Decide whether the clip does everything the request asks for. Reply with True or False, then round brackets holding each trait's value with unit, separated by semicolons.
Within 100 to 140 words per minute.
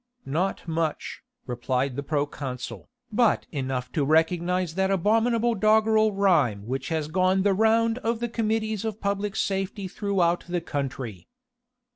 True (135 wpm)